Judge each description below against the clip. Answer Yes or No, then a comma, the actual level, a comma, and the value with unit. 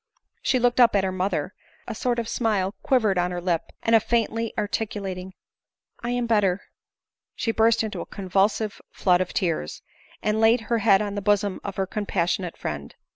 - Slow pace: No, average, 180 wpm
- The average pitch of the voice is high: Yes, high, 205 Hz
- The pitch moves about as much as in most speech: Yes, average, 3.3 semitones